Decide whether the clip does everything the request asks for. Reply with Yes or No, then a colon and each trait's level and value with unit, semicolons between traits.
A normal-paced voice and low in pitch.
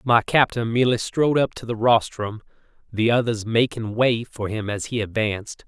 Yes: average, 180 wpm; low, 115 Hz